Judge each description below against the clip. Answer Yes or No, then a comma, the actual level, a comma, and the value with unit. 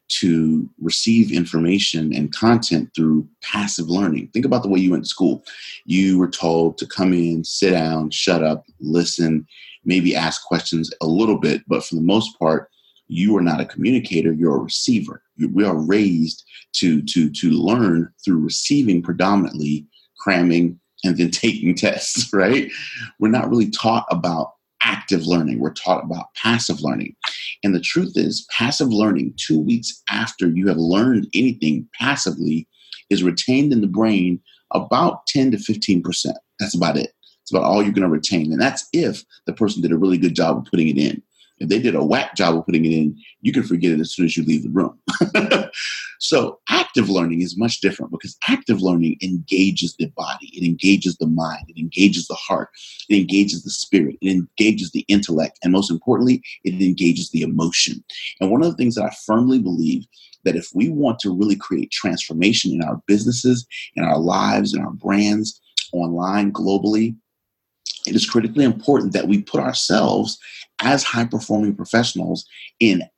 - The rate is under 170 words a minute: No, average, 180 wpm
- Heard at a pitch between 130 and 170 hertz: No, very low, 90 Hz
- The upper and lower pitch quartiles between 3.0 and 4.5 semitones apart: Yes, average, 3.9 semitones